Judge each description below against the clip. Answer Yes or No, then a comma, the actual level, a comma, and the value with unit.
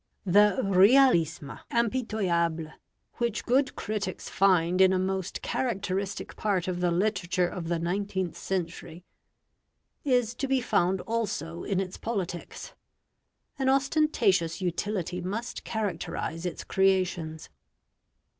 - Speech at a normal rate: No, slow, 110 wpm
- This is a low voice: No, high, 190 Hz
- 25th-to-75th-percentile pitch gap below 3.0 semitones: No, average, 3.8 semitones